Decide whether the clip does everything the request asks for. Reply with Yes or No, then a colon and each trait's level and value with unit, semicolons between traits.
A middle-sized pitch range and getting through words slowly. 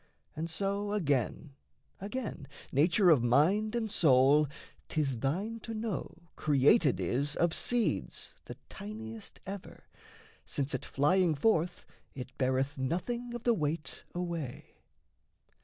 No: wide, 6.8 semitones; slow, 120 wpm